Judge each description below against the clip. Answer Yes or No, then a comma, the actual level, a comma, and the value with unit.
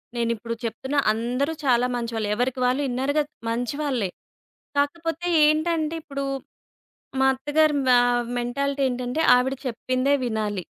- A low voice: No, very high, 255 Hz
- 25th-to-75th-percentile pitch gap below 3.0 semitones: No, average, 3.3 semitones